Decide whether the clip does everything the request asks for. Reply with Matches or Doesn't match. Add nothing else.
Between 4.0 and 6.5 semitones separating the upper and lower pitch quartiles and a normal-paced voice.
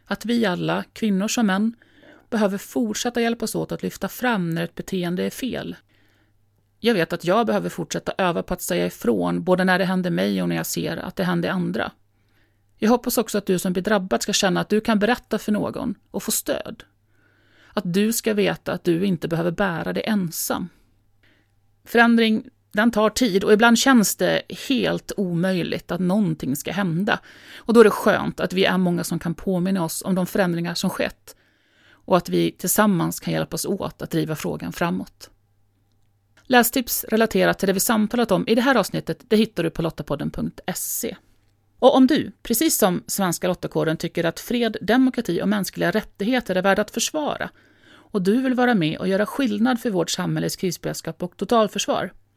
Matches